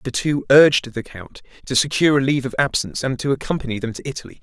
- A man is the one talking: Yes, male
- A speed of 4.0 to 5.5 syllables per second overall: No, 7.0 syllables/s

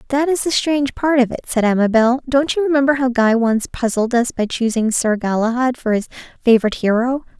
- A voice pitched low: No, high, 245 Hz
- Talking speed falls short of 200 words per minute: No, fast, 205 wpm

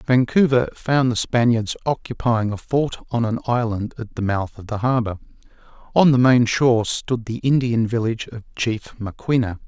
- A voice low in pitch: Yes, low, 115 Hz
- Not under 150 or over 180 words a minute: Yes, average, 165 wpm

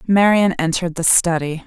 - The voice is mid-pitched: Yes, medium, 175 Hz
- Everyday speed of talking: Yes, average, 145 wpm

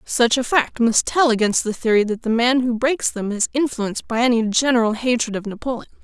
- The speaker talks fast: Yes, fast, 220 wpm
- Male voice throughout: No, female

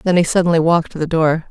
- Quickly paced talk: Yes, fast, 280 wpm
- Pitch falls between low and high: Yes, medium, 165 Hz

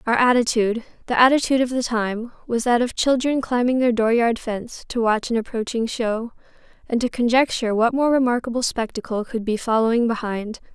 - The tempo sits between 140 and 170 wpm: Yes, average, 160 wpm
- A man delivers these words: No, female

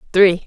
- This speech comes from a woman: Yes, female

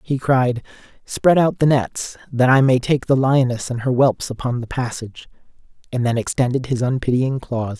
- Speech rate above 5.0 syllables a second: No, 4.9 syllables/s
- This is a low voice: Yes, low, 125 Hz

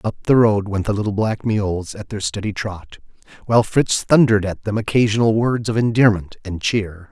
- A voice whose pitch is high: No, low, 105 Hz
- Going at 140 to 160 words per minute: No, average, 195 wpm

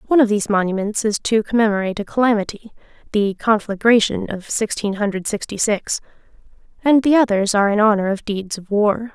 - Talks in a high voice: Yes, high, 210 Hz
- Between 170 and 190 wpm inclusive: No, average, 155 wpm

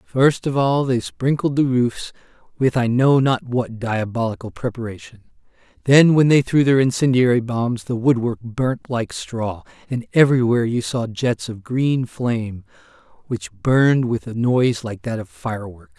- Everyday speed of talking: Yes, average, 160 wpm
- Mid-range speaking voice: No, low, 120 Hz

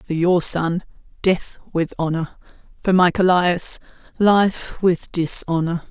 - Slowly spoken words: Yes, slow, 120 wpm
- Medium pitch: Yes, medium, 175 Hz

